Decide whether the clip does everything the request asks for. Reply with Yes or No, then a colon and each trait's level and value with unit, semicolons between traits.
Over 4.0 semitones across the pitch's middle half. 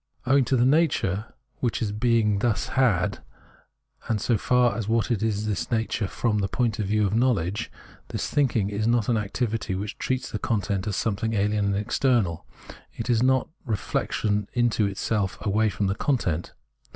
No: average, 2.9 semitones